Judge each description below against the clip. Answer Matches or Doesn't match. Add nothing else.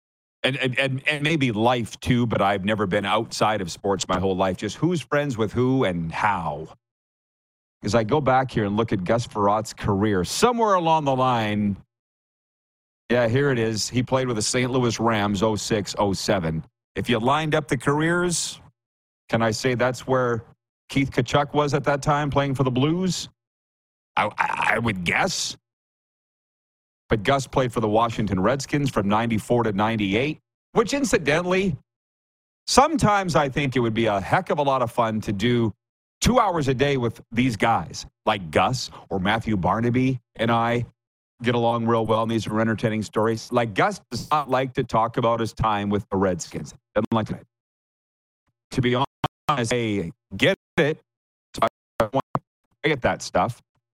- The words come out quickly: Doesn't match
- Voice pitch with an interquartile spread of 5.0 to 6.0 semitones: Doesn't match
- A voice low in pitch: Matches